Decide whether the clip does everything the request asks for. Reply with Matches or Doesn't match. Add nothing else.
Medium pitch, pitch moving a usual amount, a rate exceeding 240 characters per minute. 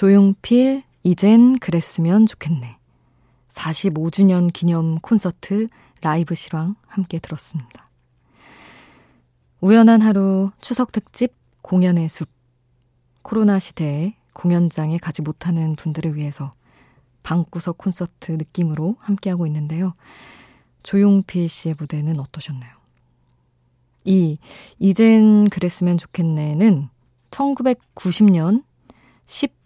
Doesn't match